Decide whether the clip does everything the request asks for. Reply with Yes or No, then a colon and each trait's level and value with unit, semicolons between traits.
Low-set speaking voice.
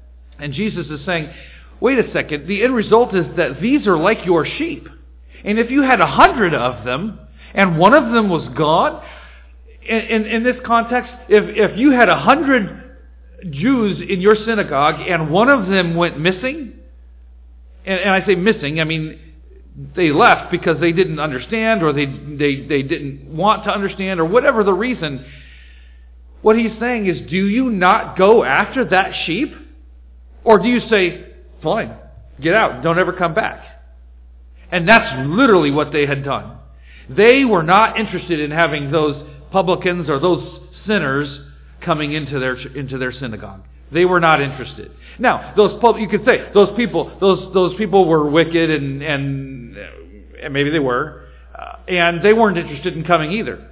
No: medium, 170 Hz